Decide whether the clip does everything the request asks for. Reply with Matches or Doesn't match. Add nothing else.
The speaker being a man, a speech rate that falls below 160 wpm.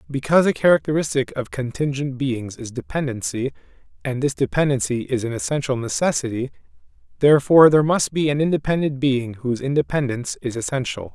Matches